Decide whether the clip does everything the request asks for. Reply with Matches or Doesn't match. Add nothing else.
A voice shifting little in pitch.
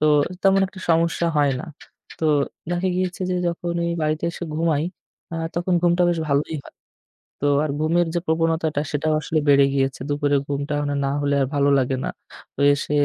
Doesn't match